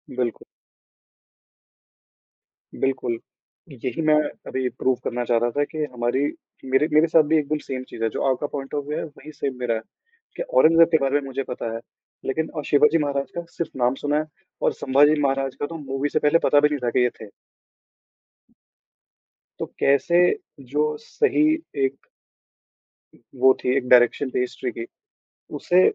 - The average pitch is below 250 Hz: Yes, medium, 140 Hz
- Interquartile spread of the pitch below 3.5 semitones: Yes, average, 2.9 semitones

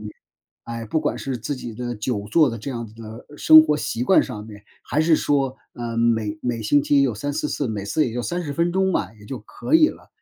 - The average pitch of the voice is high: No, low, 125 Hz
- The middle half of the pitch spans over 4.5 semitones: Yes, average, 4.9 semitones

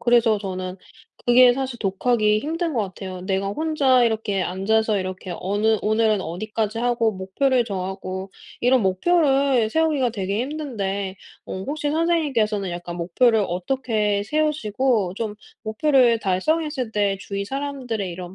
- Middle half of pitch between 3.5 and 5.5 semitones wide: Yes, average, 5.1 semitones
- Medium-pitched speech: No, high, 220 Hz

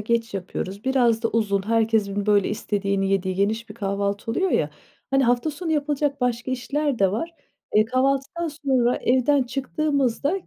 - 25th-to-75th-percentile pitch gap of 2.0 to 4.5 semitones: No, average, 5.1 semitones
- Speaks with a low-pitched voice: No, high, 235 Hz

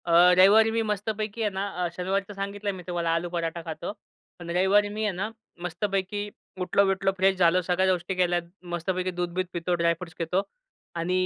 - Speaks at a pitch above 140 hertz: Yes, medium, 185 Hz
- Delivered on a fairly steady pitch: Yes, narrow, 2.3 semitones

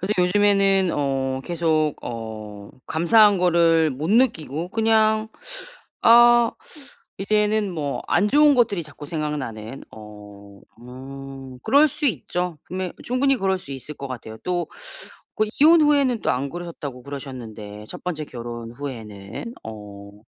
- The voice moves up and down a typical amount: No, wide, 8.5 semitones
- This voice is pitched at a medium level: Yes, medium, 160 Hz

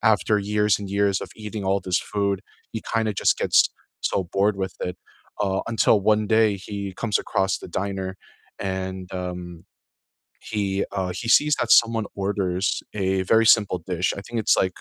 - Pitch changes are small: Yes, narrow, 2.0 semitones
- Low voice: Yes, low, 100 Hz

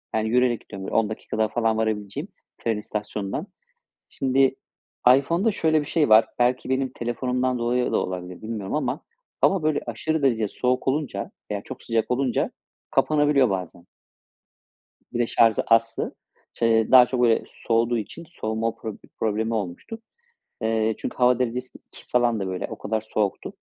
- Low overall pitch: Yes, low, 115 Hz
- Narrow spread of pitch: No, average, 3.0 semitones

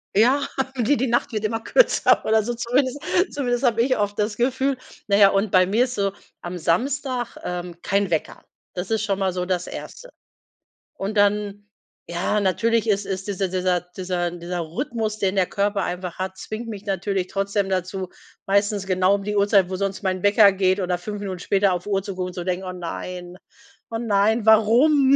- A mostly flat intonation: No, average, 3.1 semitones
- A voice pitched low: No, high, 200 Hz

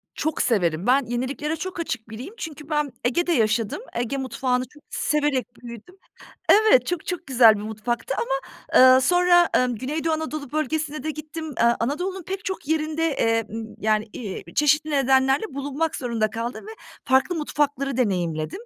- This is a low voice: No, very high, 275 Hz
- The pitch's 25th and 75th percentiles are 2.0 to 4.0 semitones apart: No, average, 4.8 semitones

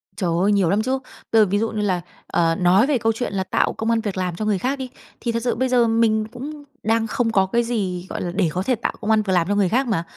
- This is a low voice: No, high, 215 Hz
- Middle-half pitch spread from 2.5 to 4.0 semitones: Yes, average, 3.7 semitones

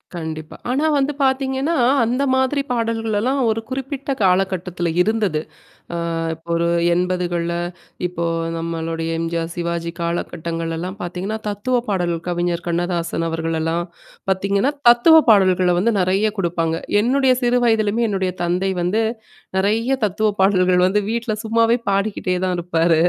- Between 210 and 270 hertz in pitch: No, medium, 185 Hz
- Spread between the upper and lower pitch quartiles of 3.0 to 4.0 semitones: No, average, 4.8 semitones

